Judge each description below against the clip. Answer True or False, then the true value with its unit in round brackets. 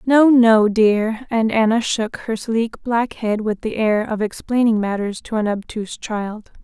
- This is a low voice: False (220 Hz)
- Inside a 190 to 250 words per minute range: False (180 wpm)